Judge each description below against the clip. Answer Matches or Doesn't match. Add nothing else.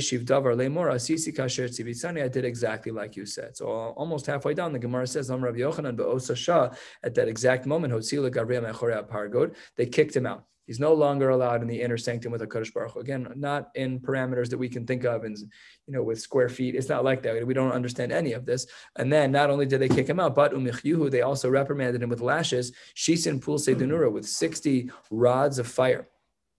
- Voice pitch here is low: Matches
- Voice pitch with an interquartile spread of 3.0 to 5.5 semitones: Doesn't match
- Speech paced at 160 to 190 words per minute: Matches